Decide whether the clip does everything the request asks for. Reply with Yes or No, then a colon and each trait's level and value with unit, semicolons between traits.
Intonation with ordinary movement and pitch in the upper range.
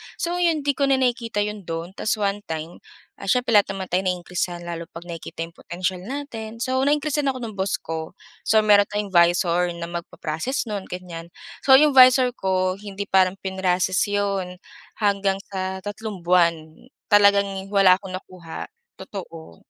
Yes: average, 3.6 semitones; high, 195 Hz